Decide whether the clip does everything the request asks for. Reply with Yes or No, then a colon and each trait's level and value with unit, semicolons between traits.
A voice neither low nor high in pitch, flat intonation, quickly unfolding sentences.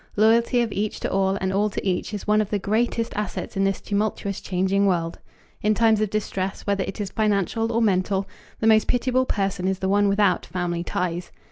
No: high, 200 Hz; narrow, 2.1 semitones; fast, 210 wpm